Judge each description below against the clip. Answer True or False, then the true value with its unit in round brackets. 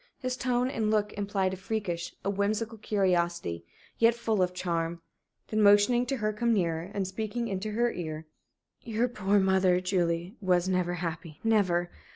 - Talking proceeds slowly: False (170 wpm)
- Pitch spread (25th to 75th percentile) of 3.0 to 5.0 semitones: True (3.7 semitones)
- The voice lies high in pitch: True (195 Hz)